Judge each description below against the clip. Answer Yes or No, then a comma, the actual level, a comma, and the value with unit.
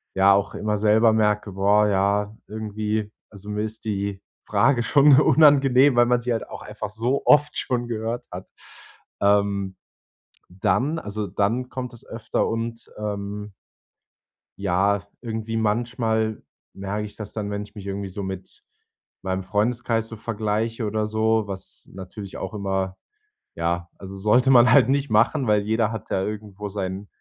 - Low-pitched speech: Yes, low, 105 Hz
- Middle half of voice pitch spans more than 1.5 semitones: Yes, narrow, 2.4 semitones